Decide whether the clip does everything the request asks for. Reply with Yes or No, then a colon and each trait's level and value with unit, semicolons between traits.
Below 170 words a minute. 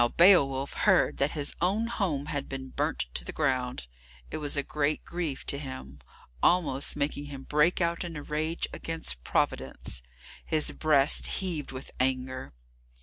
Yes: average, 160 wpm